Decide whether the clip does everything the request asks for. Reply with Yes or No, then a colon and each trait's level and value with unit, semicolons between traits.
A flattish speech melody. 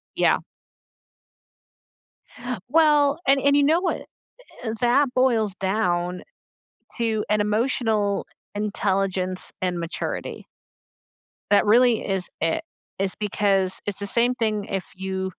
No: average, 4.4 semitones